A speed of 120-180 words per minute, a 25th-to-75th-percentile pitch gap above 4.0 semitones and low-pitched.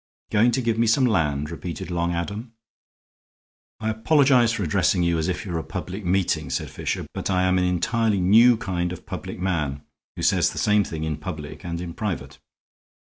No: average, 195 wpm; average, 4.4 semitones; very low, 90 Hz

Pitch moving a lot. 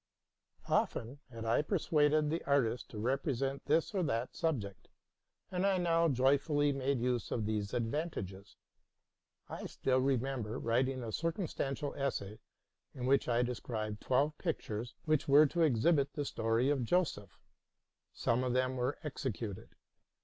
No: average, 4.3 semitones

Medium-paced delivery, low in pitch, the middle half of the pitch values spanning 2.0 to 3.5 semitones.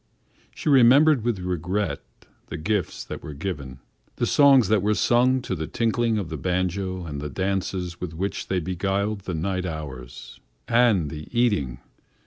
No: average, 160 wpm; very low, 95 Hz; wide, 5.4 semitones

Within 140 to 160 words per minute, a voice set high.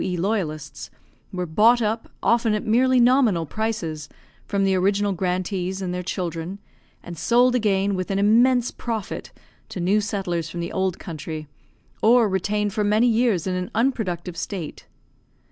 Yes: average, 155 wpm; high, 195 Hz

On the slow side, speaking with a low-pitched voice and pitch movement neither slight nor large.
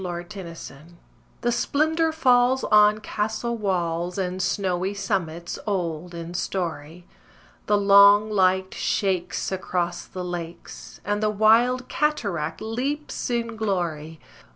No: slow, 125 wpm; high, 195 Hz; average, 4.0 semitones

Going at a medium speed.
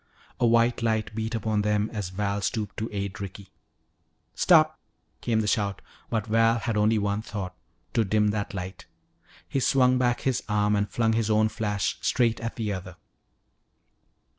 Yes: average, 165 wpm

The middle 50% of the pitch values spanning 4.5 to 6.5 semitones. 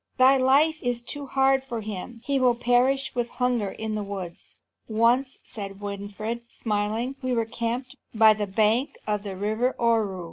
No: average, 3.4 semitones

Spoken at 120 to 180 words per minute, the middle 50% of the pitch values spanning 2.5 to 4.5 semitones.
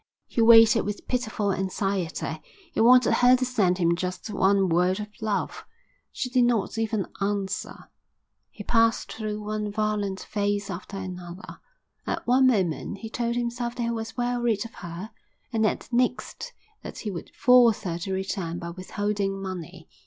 Yes: average, 165 wpm; average, 3.5 semitones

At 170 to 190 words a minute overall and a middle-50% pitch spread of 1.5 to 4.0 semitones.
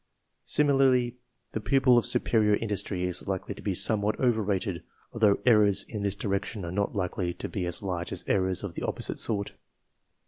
Yes: average, 180 wpm; average, 3.1 semitones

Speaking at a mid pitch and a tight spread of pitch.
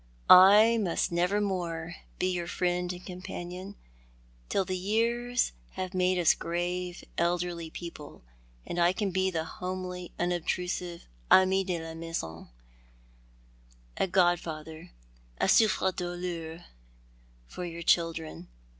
Yes: medium, 175 Hz; narrow, 1.9 semitones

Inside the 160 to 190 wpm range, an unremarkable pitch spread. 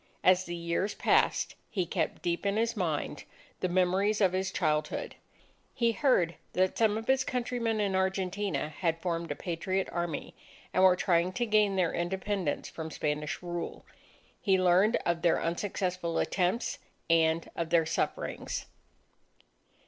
No: average, 150 wpm; average, 3.1 semitones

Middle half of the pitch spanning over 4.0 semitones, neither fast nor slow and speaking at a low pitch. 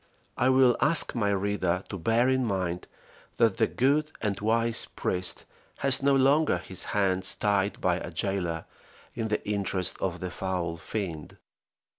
Yes: average, 4.5 semitones; average, 155 wpm; low, 100 Hz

